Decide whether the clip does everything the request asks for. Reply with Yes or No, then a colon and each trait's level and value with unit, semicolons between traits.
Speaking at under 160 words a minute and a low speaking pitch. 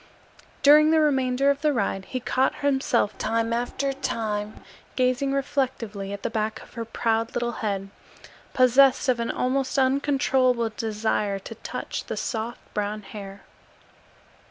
No: average, 140 wpm; high, 240 Hz